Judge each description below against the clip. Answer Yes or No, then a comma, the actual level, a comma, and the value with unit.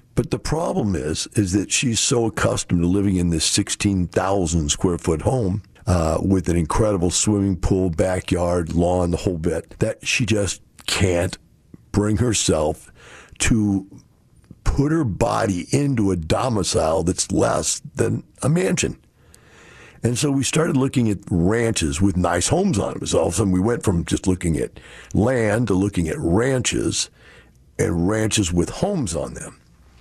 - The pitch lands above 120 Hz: No, very low, 95 Hz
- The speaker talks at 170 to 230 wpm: No, average, 160 wpm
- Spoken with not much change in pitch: No, average, 3.9 semitones